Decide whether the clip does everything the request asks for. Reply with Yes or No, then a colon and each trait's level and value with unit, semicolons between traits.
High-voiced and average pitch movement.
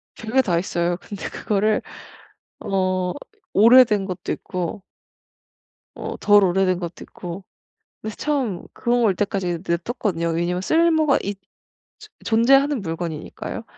Yes: high, 195 Hz; average, 4.5 semitones